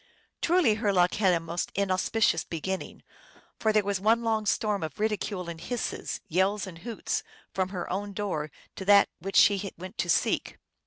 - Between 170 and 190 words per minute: Yes, average, 175 wpm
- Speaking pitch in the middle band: No, high, 195 Hz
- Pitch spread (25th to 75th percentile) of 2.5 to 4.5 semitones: Yes, average, 2.8 semitones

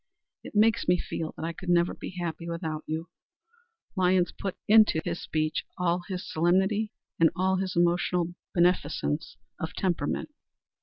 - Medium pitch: Yes, medium, 175 Hz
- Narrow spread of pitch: Yes, narrow, 2.3 semitones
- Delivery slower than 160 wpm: Yes, average, 150 wpm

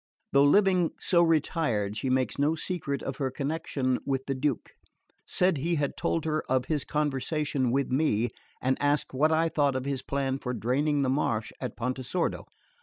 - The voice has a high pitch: No, medium, 140 Hz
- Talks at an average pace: Yes, average, 180 wpm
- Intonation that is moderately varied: Yes, average, 3.1 semitones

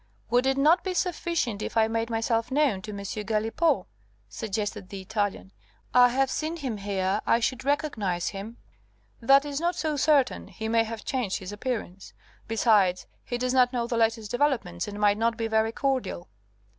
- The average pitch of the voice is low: No, high, 230 Hz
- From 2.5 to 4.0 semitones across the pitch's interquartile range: No, average, 4.5 semitones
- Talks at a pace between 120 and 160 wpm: No, average, 180 wpm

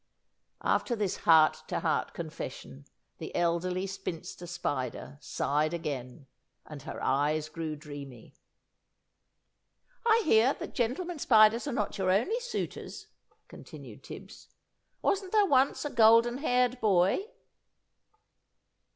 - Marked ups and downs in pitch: Yes, wide, 8.3 semitones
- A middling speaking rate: No, slow, 115 wpm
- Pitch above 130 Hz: Yes, high, 190 Hz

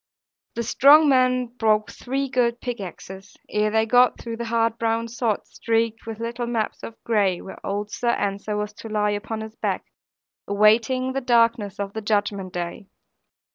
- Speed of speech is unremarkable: Yes, average, 170 wpm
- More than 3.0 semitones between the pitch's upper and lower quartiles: No, narrow, 2.4 semitones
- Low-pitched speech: No, high, 225 Hz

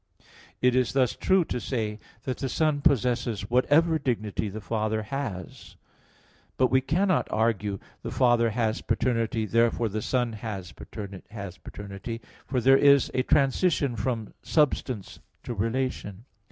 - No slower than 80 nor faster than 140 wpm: Yes, slow, 135 wpm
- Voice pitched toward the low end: Yes, low, 120 Hz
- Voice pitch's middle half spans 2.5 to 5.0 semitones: Yes, average, 3.7 semitones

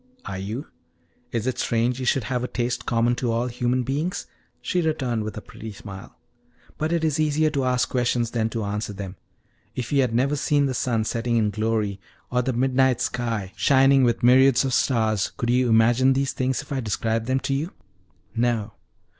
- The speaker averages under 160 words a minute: No, average, 195 wpm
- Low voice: Yes, low, 120 Hz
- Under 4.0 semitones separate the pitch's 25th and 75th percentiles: Yes, average, 2.9 semitones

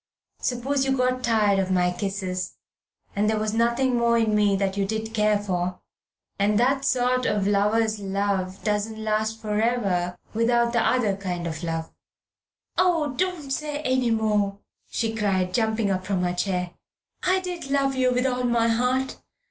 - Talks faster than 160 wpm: Yes, average, 170 wpm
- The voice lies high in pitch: Yes, high, 220 Hz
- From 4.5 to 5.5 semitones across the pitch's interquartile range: No, average, 4.1 semitones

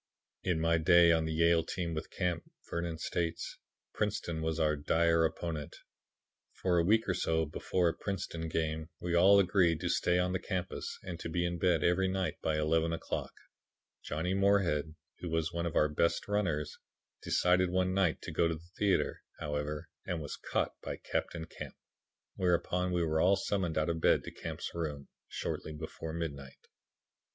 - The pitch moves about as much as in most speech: No, narrow, 2.1 semitones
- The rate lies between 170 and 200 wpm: Yes, average, 180 wpm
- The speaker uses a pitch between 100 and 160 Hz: No, very low, 85 Hz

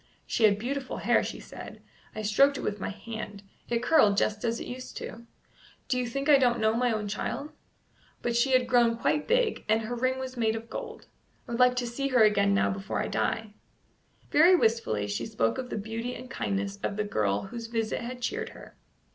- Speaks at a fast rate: Yes, fast, 220 wpm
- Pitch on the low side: No, high, 230 Hz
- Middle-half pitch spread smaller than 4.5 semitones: Yes, average, 3.1 semitones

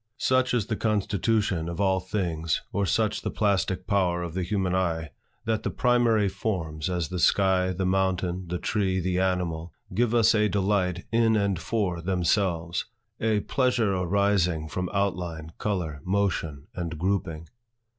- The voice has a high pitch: No, very low, 95 Hz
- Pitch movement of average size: Yes, average, 3.0 semitones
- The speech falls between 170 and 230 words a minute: No, average, 155 wpm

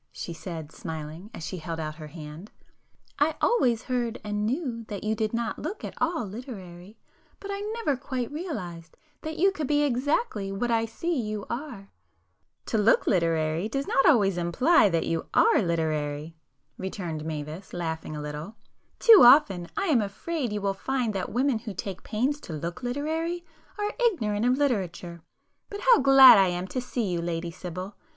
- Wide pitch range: Yes, wide, 7.9 semitones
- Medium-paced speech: Yes, average, 175 wpm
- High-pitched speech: Yes, high, 210 Hz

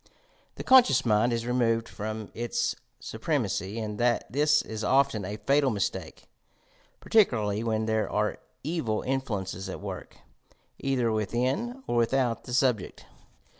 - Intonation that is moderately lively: Yes, average, 3.7 semitones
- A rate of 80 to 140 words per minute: Yes, slow, 135 wpm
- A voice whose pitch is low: Yes, low, 115 Hz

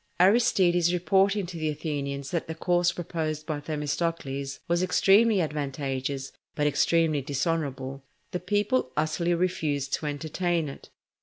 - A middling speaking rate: No, slow, 130 wpm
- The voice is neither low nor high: Yes, medium, 160 Hz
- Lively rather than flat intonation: No, average, 3.7 semitones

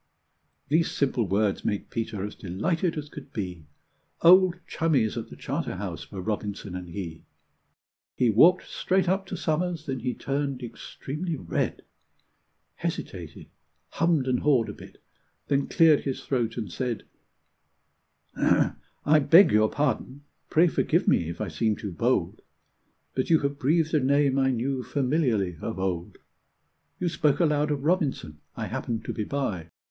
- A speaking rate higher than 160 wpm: No, average, 150 wpm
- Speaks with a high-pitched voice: No, low, 130 Hz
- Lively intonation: Yes, wide, 6.6 semitones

